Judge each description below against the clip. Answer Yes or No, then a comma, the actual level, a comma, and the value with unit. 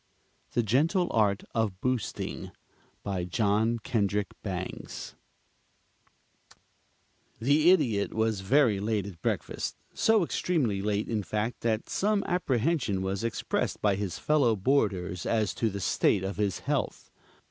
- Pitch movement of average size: Yes, average, 4.4 semitones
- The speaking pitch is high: No, low, 110 Hz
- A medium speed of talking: No, slow, 125 wpm